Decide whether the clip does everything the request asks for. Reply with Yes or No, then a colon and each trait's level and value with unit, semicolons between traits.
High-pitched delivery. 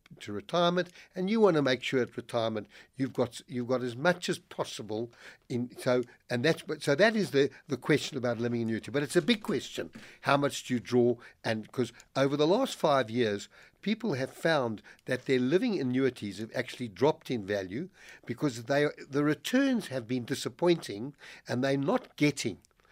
No: low, 130 Hz